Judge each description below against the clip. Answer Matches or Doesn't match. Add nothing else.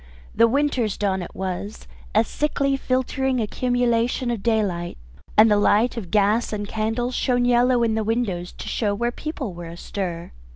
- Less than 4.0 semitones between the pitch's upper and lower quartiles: Matches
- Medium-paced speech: Matches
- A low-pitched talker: Doesn't match